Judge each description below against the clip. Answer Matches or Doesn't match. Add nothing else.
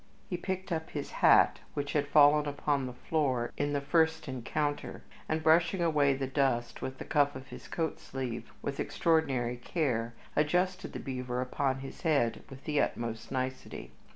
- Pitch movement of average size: Matches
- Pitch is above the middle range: Doesn't match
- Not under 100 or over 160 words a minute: Doesn't match